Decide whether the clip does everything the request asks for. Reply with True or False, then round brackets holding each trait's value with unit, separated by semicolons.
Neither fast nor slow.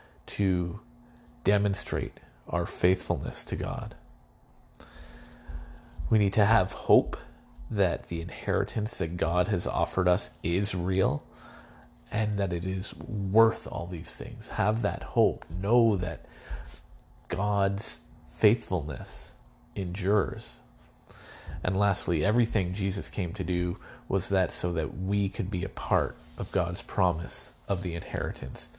False (125 wpm)